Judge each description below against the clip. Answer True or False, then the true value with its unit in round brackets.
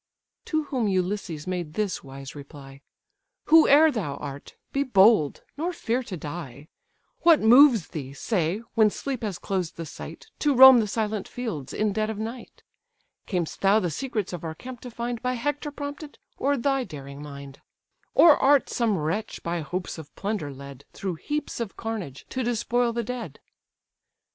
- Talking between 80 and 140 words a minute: False (170 wpm)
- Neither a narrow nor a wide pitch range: False (7.9 semitones)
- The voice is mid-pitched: False (215 Hz)